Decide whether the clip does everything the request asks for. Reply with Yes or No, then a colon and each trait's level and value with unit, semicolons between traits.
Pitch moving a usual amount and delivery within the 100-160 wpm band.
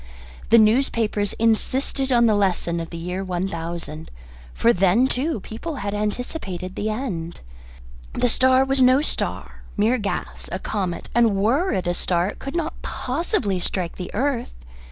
No: wide, 5.7 semitones; average, 155 wpm